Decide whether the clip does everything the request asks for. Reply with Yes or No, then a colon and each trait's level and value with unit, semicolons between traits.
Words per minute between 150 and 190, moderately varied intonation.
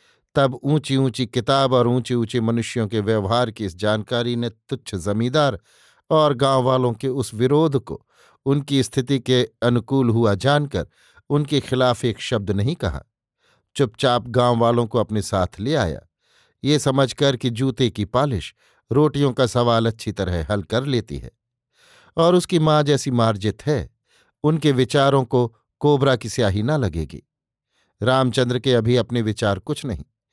Yes: average, 155 wpm; average, 3.5 semitones